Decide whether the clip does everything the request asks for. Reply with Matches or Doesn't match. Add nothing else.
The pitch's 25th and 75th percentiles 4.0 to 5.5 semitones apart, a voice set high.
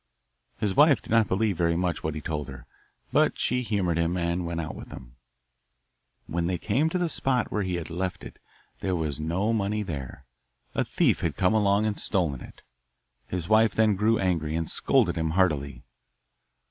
Doesn't match